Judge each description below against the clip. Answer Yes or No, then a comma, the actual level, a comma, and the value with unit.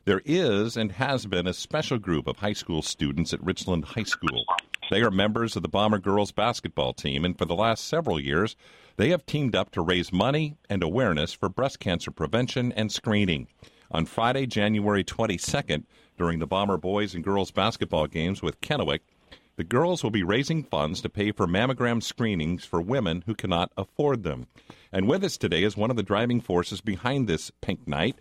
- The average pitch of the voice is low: Yes, low, 105 Hz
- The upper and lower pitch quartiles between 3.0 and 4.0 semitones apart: No, average, 4.8 semitones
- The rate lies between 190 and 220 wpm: Yes, average, 195 wpm